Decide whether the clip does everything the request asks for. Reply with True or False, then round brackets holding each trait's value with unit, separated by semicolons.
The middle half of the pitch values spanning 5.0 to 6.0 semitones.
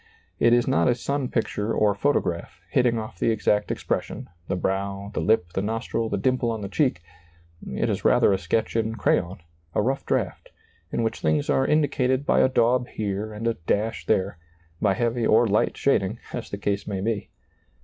False (3.4 semitones)